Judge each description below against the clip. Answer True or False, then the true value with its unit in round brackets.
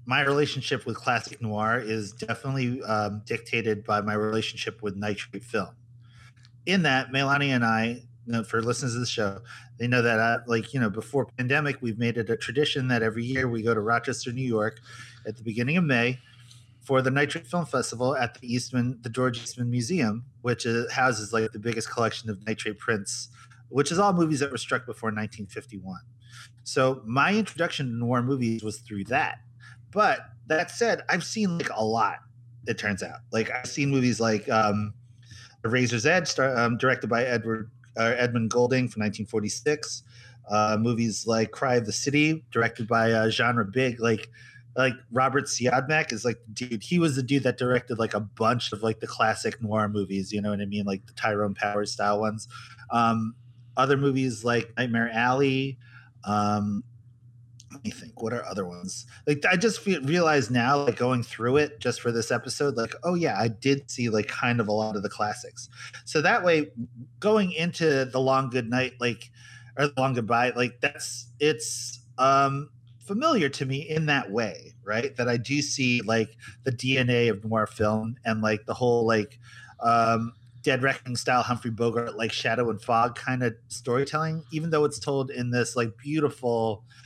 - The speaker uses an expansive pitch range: False (2.5 semitones)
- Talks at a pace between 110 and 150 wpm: False (190 wpm)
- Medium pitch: False (120 Hz)